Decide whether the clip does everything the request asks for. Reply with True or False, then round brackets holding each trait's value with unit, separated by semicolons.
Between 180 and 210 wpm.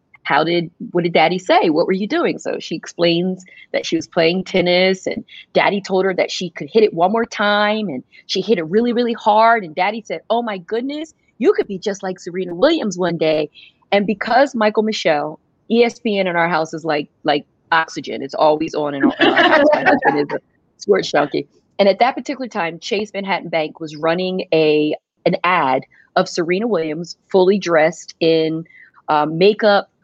True (195 wpm)